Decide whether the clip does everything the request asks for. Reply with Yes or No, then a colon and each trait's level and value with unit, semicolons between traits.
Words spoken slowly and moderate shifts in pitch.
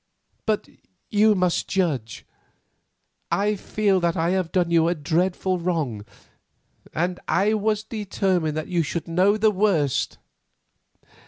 Yes: slow, 130 wpm; average, 3.5 semitones